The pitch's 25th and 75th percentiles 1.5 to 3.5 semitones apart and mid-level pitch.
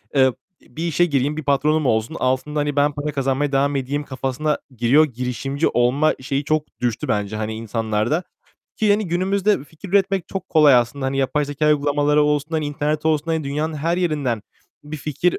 Yes: average, 2.8 semitones; medium, 145 Hz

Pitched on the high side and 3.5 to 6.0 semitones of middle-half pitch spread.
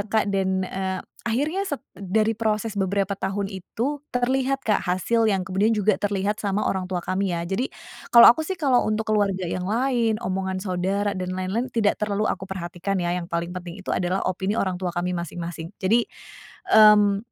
No: high, 195 Hz; average, 2.8 semitones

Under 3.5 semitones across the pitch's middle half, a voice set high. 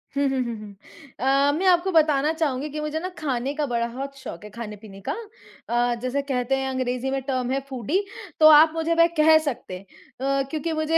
No: average, 4.1 semitones; very high, 275 Hz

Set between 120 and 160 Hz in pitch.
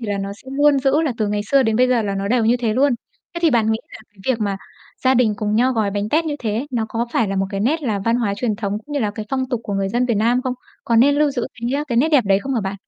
No: high, 230 Hz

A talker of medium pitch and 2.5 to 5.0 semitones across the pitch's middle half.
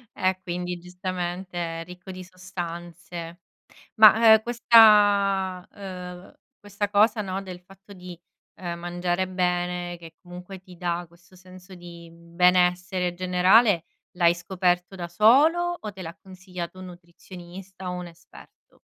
No: medium, 180 Hz; narrow, 1.5 semitones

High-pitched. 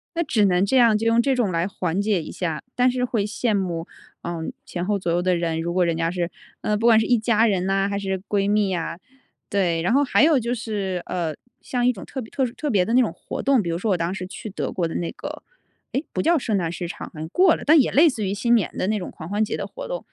Yes: high, 200 Hz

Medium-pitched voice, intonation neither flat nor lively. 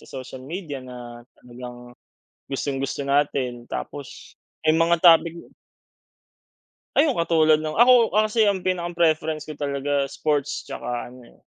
Yes: medium, 150 Hz; average, 4.5 semitones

